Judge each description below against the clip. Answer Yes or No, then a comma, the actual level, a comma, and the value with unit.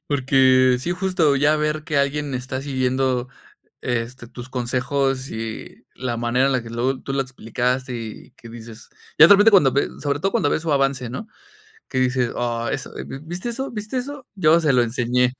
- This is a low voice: Yes, low, 130 Hz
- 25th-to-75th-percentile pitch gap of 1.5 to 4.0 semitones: Yes, average, 3.4 semitones